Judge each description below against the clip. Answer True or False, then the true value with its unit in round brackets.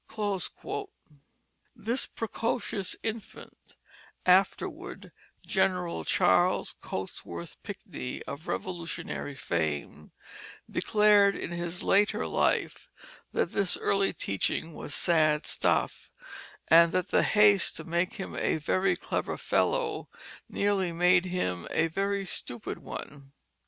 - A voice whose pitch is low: False (180 Hz)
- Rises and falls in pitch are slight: False (4.2 semitones)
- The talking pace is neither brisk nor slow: False (105 wpm)